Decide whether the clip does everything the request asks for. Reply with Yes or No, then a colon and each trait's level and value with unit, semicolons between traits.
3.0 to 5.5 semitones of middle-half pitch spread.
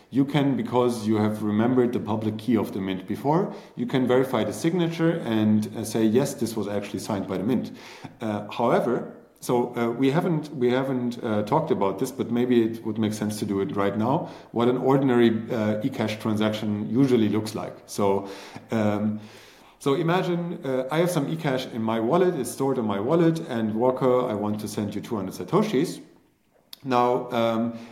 Yes: average, 3.7 semitones